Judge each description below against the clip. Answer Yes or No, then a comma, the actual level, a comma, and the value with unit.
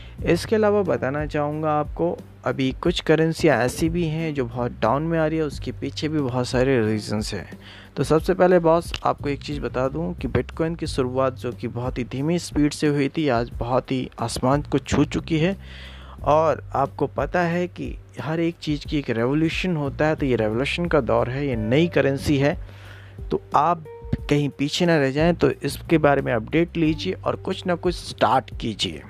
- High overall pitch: No, medium, 140 Hz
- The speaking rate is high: Yes, fast, 200 wpm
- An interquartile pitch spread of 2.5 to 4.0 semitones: No, average, 4.7 semitones